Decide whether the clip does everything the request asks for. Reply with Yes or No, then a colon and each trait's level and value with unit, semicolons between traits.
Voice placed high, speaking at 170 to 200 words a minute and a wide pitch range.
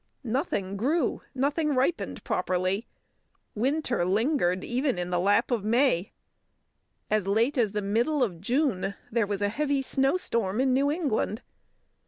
No: high, 235 Hz; average, 140 wpm; wide, 5.7 semitones